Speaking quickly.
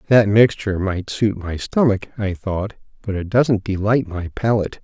No: average, 175 wpm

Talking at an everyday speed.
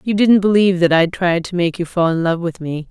No: fast, 290 wpm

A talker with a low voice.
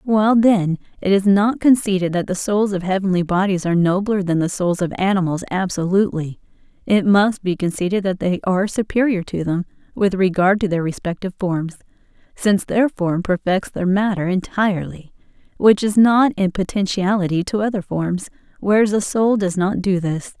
No: high, 190 Hz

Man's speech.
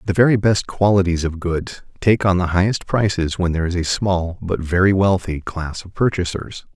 Yes: male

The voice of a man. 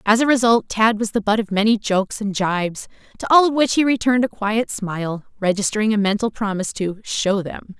No: female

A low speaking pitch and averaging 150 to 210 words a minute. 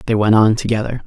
No: low, 110 Hz; fast, 225 wpm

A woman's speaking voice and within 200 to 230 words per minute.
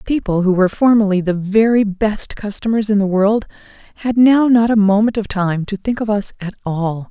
Yes: female; fast, 205 wpm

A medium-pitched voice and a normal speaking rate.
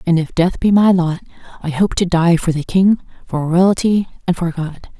No: medium, 175 Hz; fast, 215 wpm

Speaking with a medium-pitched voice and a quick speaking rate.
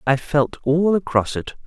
No: medium, 150 Hz; average, 180 wpm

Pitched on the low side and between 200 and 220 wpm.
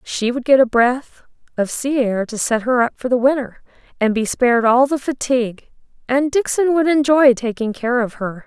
No: very high, 250 Hz; fast, 205 wpm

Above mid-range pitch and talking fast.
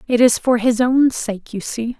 Yes: high, 240 Hz; fast, 240 wpm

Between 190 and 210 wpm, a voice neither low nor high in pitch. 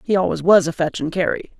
No: fast, 265 wpm; medium, 175 Hz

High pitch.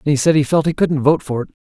No: medium, 150 Hz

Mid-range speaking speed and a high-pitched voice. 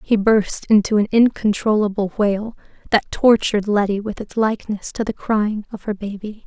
Yes: average, 165 wpm; high, 210 Hz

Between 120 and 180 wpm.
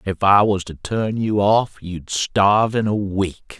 No: average, 200 wpm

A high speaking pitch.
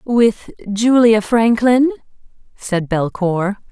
Yes: high, 220 Hz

